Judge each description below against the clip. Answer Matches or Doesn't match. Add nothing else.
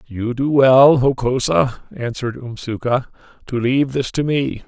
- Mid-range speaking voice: Doesn't match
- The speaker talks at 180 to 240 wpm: Doesn't match